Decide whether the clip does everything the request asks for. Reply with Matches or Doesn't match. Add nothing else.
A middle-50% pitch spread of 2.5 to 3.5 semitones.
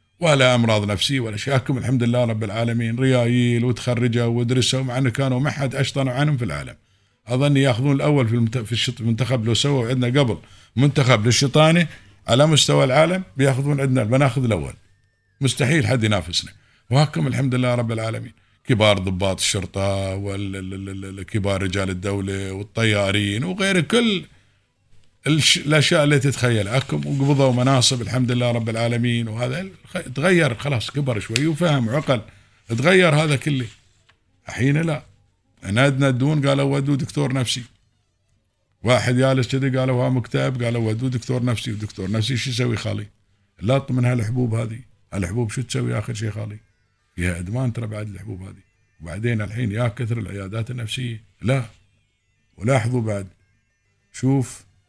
Doesn't match